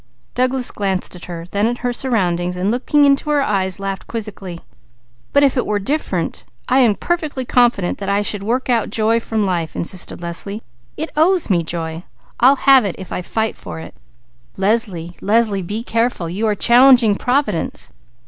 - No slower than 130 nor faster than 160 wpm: No, average, 175 wpm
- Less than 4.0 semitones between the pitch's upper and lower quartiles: No, average, 5.0 semitones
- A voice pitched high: Yes, high, 215 Hz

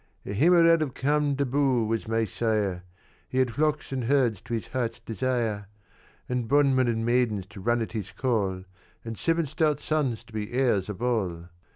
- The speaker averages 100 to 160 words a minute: No, average, 175 wpm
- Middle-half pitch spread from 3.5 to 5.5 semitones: Yes, average, 4.0 semitones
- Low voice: Yes, low, 120 Hz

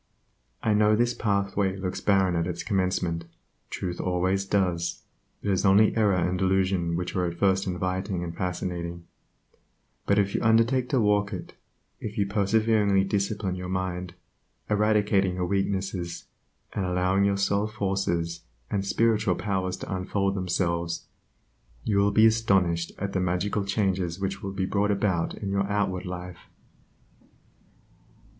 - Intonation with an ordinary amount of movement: No, narrow, 2.1 semitones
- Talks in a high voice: No, very low, 95 Hz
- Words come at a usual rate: Yes, average, 145 wpm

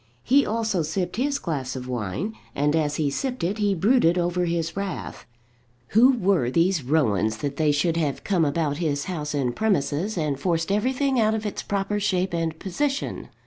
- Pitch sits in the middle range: Yes, medium, 170 Hz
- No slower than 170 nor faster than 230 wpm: Yes, average, 185 wpm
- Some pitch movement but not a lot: No, wide, 5.8 semitones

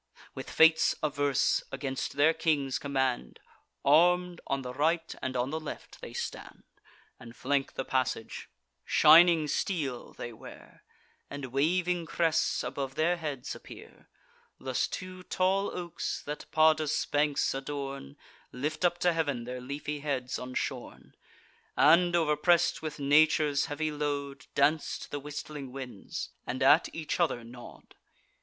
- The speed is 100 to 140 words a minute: Yes, slow, 135 wpm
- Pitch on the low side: No, medium, 145 Hz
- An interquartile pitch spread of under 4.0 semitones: Yes, average, 3.2 semitones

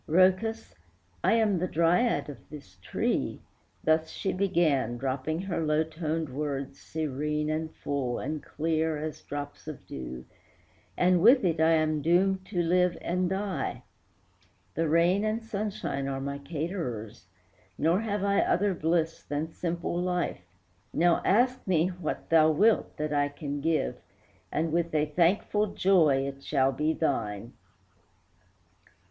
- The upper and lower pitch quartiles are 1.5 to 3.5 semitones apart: No, average, 3.9 semitones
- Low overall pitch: No, medium, 160 Hz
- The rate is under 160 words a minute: Yes, average, 140 wpm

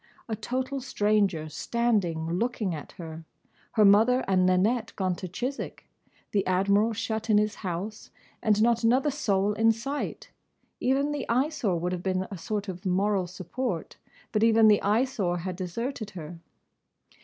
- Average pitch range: Yes, average, 4.2 semitones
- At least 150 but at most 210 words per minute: Yes, average, 155 wpm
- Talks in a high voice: Yes, high, 210 Hz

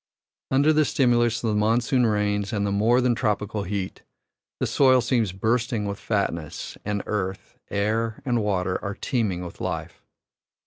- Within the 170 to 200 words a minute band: No, average, 160 wpm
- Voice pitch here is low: Yes, low, 105 Hz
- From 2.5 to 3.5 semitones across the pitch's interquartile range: Yes, average, 3.0 semitones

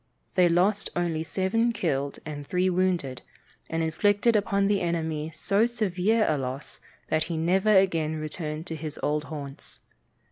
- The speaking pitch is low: No, medium, 170 Hz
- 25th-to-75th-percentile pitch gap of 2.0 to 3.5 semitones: No, average, 4.2 semitones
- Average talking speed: Yes, average, 150 wpm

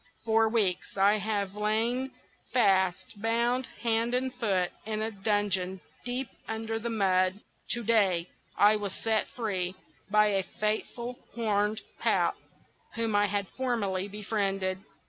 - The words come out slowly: Yes, slow, 130 wpm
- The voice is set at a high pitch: Yes, high, 210 Hz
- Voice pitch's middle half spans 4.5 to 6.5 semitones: No, narrow, 2.6 semitones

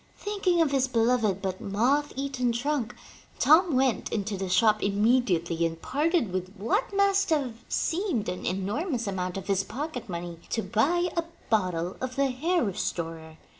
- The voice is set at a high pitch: Yes, high, 235 Hz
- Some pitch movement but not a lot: No, wide, 7.4 semitones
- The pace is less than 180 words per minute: Yes, average, 165 wpm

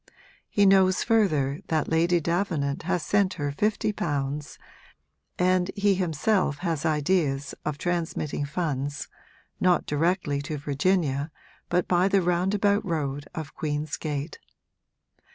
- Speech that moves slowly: Yes, slow, 120 wpm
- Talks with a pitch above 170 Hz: No, medium, 165 Hz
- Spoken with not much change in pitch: No, average, 4.2 semitones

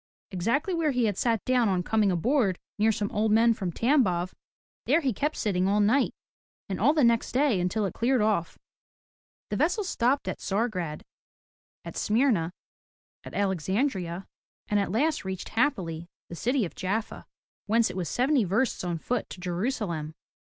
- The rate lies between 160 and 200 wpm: Yes, average, 170 wpm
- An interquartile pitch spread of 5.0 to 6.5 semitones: Yes, average, 5.3 semitones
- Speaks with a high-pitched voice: Yes, high, 215 Hz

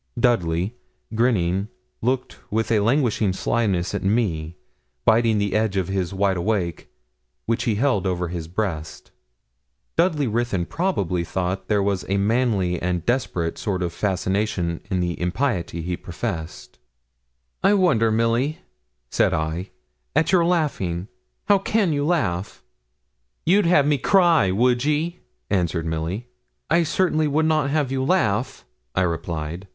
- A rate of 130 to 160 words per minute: Yes, average, 140 wpm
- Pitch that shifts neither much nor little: No, wide, 7.0 semitones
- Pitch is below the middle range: Yes, low, 105 Hz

